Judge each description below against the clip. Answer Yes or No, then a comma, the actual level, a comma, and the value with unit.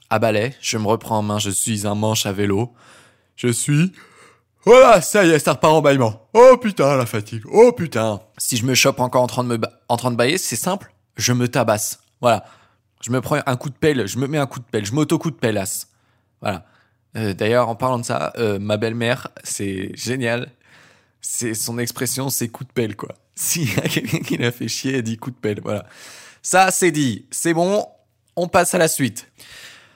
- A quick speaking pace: Yes, fast, 225 wpm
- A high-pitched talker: No, low, 120 Hz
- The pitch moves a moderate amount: Yes, average, 4.0 semitones